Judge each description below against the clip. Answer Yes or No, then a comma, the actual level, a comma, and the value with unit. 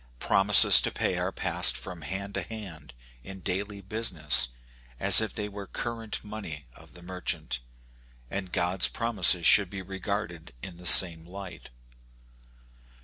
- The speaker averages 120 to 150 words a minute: Yes, average, 145 wpm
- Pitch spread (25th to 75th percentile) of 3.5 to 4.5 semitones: No, average, 2.8 semitones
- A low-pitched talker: Yes, very low, 95 Hz